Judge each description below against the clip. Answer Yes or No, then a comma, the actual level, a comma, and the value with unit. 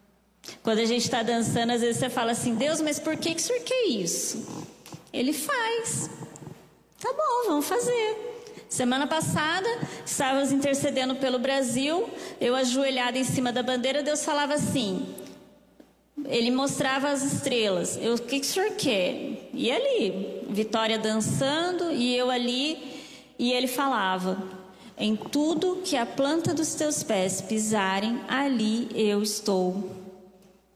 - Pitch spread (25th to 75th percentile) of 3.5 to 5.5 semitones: Yes, average, 4.8 semitones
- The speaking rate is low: No, average, 140 wpm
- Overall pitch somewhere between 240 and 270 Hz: Yes, very high, 260 Hz